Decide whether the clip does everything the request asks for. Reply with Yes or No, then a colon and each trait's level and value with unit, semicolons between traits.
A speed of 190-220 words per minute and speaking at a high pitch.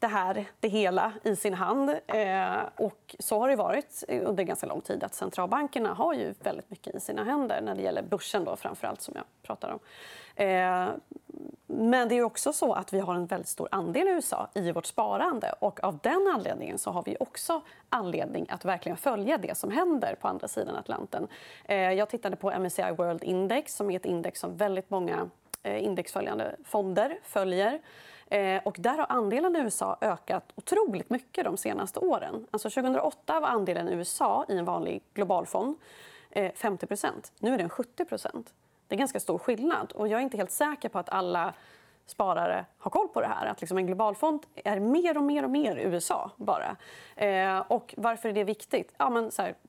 Yes: fast, 195 wpm; high, 220 Hz